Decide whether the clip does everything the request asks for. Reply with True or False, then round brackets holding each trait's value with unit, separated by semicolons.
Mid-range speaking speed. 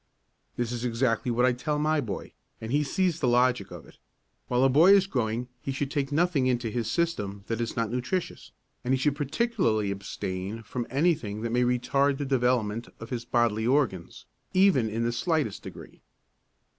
True (185 wpm)